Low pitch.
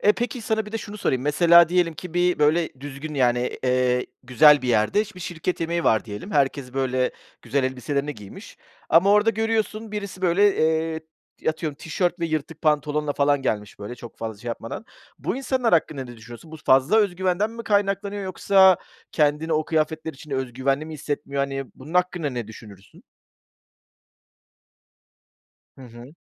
No: medium, 155 Hz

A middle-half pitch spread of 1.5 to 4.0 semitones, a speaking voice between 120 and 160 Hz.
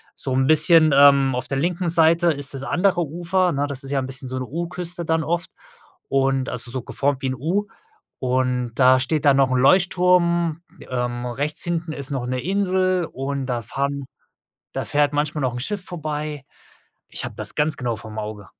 No: average, 4.6 semitones; medium, 140 Hz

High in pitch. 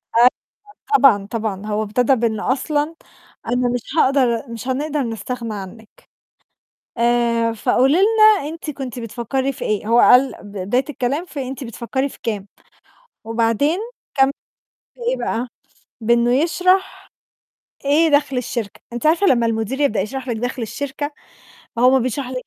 Yes: very high, 250 Hz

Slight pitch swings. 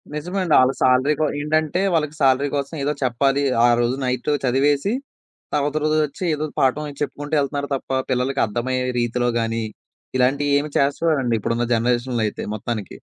No: average, 3.1 semitones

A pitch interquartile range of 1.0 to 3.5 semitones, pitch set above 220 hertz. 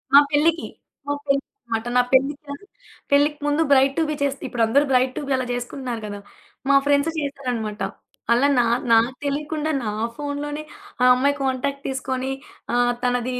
Yes: narrow, 2.6 semitones; very high, 275 Hz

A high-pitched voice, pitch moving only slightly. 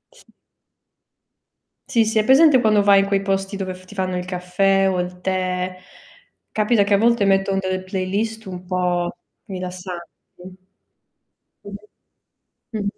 Yes: high, 195 Hz; narrow, 1.8 semitones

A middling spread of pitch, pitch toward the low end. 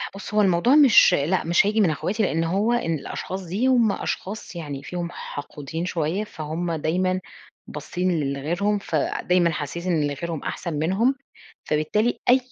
No: average, 4.5 semitones; medium, 175 Hz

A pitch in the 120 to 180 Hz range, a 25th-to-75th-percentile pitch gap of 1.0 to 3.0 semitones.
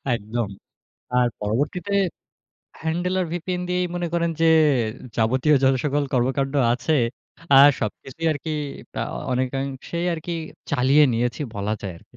No: medium, 140 Hz; average, 5.1 semitones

